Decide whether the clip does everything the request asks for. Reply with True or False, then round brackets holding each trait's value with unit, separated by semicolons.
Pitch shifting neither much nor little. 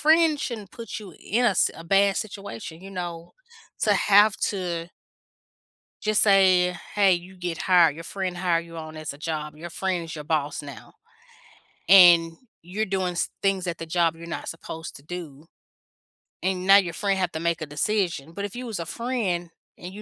True (3.0 semitones)